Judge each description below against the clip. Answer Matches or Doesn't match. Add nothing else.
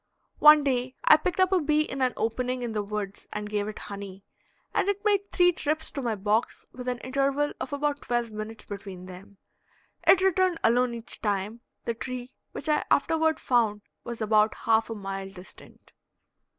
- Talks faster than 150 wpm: Matches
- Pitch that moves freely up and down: Matches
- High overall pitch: Matches